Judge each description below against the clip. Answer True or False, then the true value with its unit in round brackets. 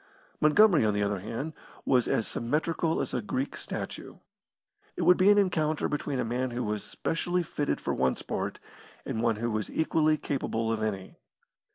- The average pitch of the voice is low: True (130 Hz)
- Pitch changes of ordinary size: False (6.2 semitones)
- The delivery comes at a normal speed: True (180 wpm)